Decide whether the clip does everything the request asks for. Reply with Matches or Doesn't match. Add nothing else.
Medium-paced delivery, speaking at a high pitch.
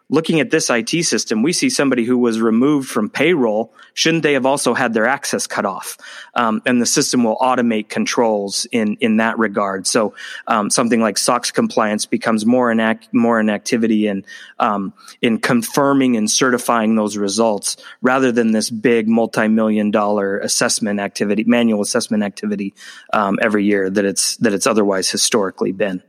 Doesn't match